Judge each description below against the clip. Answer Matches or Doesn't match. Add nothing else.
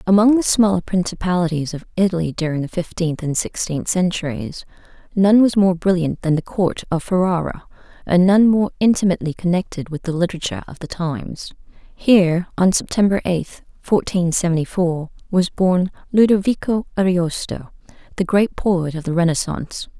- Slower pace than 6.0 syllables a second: Matches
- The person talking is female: Matches